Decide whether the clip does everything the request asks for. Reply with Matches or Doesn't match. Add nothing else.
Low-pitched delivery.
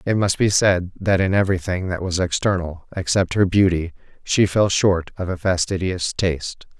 Matches